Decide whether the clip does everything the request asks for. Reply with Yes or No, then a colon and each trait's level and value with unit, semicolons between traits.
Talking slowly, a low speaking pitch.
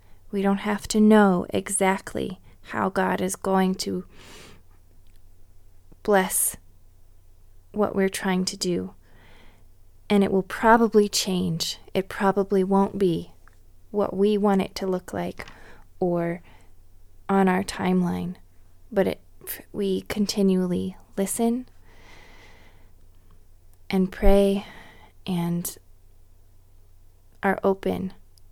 No: slow, 100 wpm; medium, 165 Hz